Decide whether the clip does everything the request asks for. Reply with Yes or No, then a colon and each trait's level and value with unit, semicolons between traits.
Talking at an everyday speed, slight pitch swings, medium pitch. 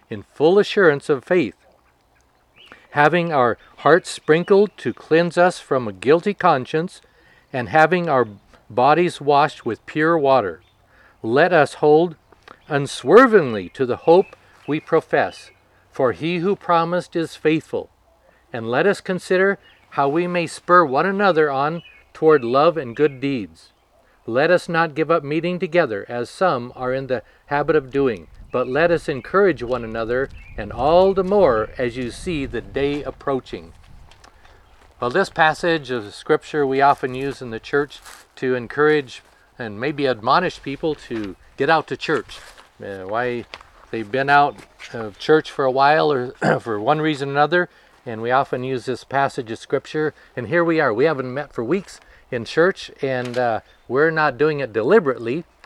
No: average, 160 wpm; average, 4.8 semitones; medium, 145 Hz